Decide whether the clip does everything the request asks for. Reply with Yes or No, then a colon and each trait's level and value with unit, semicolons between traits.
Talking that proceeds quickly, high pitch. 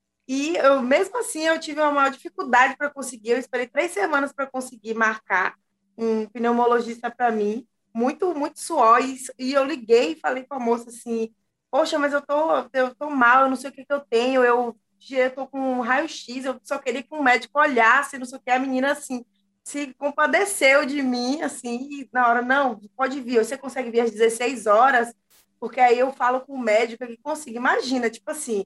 Yes: fast, 205 wpm; very high, 255 Hz